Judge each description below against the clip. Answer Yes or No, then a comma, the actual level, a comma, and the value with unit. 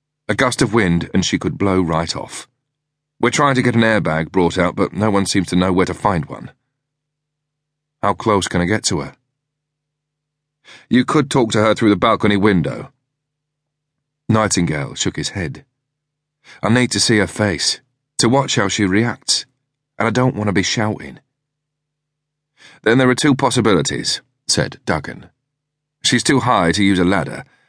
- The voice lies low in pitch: Yes, low, 130 Hz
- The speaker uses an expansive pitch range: Yes, wide, 6.2 semitones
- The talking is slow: No, average, 175 wpm